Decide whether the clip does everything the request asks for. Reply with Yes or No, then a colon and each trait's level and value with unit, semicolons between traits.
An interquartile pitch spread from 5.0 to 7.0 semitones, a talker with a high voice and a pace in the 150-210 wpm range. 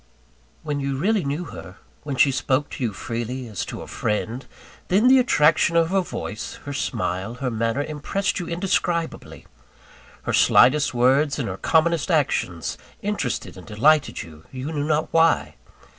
No: wide, 5.6 semitones; medium, 145 Hz; average, 160 wpm